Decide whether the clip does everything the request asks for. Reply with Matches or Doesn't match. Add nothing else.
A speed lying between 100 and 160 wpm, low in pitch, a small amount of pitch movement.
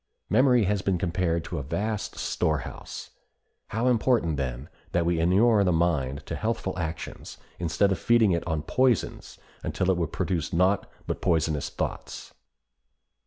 Doesn't match